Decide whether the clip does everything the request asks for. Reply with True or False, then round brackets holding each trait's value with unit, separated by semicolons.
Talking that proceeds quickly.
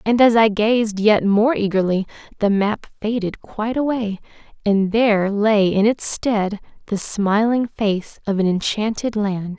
False (155 wpm)